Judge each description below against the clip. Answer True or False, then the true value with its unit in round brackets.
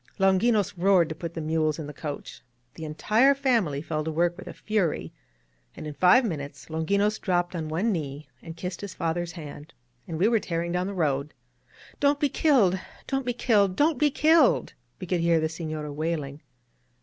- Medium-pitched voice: True (175 Hz)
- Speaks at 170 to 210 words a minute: True (195 wpm)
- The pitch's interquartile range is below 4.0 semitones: False (4.9 semitones)